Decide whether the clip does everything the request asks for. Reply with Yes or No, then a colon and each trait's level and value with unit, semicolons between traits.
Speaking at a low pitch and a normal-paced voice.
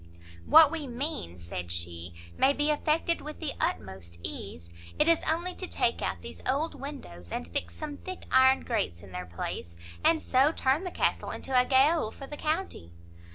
No: very high, 265 Hz; average, 185 wpm